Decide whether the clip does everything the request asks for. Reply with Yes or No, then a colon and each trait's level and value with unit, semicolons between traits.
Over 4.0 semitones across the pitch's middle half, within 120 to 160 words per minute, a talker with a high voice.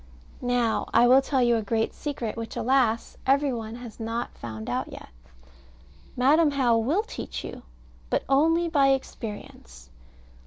No: average, 3.4 semitones; average, 150 wpm; high, 245 Hz